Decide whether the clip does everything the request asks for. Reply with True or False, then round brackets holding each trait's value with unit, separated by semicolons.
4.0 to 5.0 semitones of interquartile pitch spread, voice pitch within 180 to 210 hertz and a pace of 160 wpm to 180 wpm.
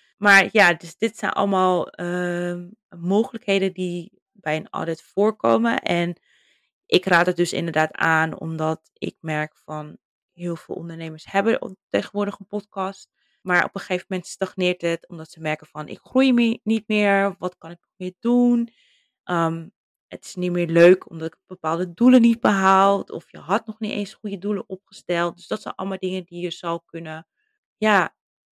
False (3.4 semitones; 185 Hz; 175 wpm)